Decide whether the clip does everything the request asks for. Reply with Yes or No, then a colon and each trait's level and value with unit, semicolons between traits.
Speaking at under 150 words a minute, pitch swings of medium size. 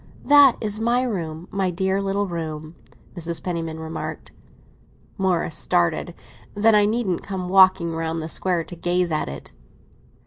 Yes: average, 140 wpm; average, 3.4 semitones